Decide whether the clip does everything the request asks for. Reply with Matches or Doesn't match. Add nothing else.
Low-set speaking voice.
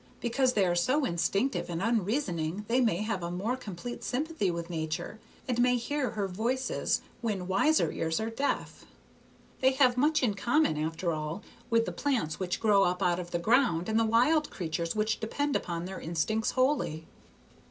Doesn't match